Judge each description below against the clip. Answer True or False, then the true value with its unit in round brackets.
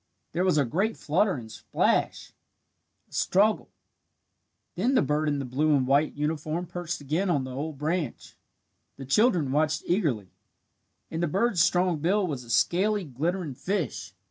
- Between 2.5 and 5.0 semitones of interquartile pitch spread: True (4.5 semitones)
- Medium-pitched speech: True (155 Hz)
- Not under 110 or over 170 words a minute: True (160 wpm)